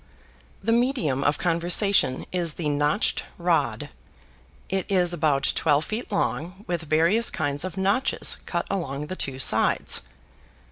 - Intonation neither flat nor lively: Yes, average, 4.7 semitones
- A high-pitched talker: No, medium, 170 Hz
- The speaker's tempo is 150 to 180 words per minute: No, slow, 135 wpm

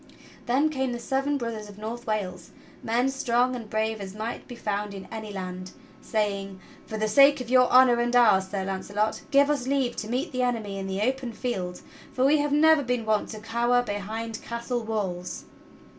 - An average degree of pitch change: Yes, average, 3.5 semitones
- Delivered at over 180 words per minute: Yes, average, 200 wpm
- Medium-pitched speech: No, high, 230 Hz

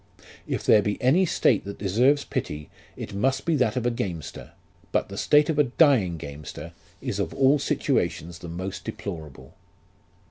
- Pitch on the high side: No, low, 105 Hz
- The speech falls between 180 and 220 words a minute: No, average, 170 wpm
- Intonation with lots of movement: Yes, wide, 7.9 semitones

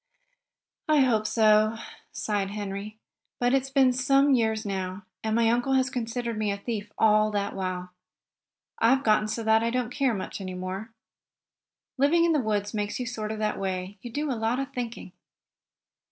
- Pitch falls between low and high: No, high, 220 Hz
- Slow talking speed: No, average, 175 wpm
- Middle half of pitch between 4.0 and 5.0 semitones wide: No, average, 3.3 semitones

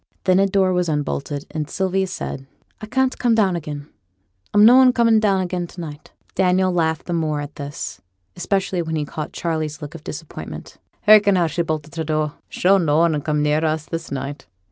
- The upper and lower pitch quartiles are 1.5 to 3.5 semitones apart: No, average, 3.9 semitones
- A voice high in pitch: No, medium, 165 Hz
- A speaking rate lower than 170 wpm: No, average, 190 wpm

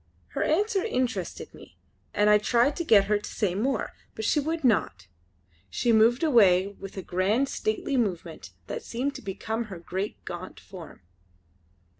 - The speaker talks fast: No, average, 165 wpm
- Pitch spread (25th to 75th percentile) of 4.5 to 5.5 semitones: Yes, average, 5.1 semitones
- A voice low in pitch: No, high, 215 Hz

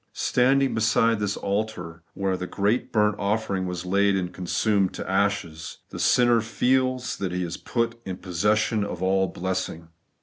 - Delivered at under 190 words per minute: Yes, average, 160 wpm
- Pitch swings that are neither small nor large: Yes, average, 3.4 semitones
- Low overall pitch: Yes, low, 100 Hz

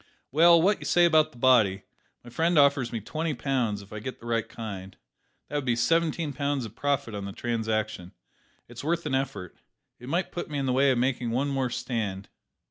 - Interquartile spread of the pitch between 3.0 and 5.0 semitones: Yes, average, 4.3 semitones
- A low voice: Yes, low, 130 Hz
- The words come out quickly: Yes, fast, 210 wpm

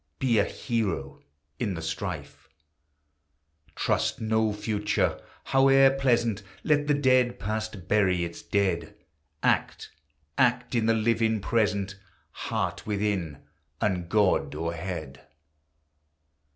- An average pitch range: Yes, average, 4.6 semitones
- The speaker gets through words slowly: Yes, slow, 110 wpm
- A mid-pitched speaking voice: No, low, 105 Hz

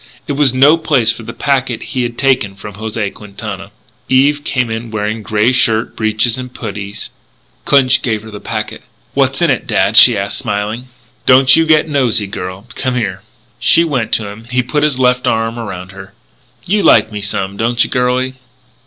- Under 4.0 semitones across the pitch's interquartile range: Yes, average, 3.6 semitones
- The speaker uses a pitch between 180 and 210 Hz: No, low, 115 Hz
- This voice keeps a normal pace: Yes, average, 190 wpm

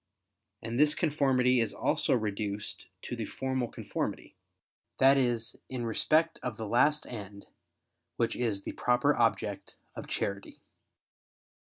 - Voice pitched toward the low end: Yes, low, 120 Hz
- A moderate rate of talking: No, slow, 130 wpm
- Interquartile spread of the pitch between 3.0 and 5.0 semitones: Yes, average, 3.5 semitones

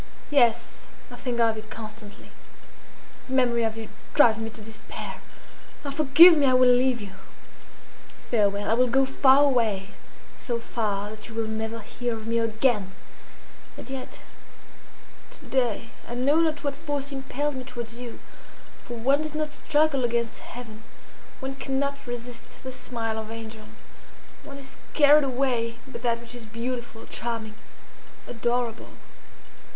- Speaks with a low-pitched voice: No, high, 240 Hz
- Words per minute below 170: Yes, average, 150 wpm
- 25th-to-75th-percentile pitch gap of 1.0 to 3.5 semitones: Yes, average, 3.1 semitones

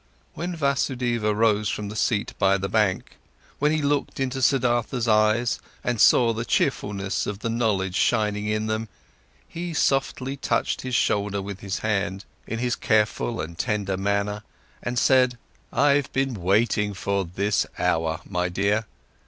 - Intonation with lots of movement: No, average, 3.6 semitones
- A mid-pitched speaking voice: No, low, 110 Hz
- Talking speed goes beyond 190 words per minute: No, average, 155 wpm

